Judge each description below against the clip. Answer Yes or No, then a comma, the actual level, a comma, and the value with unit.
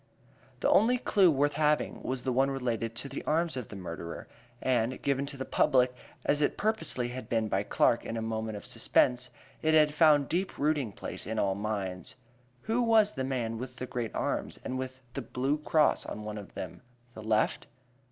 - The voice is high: No, low, 130 Hz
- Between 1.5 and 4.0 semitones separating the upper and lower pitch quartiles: No, average, 4.9 semitones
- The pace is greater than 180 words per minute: Yes, average, 200 wpm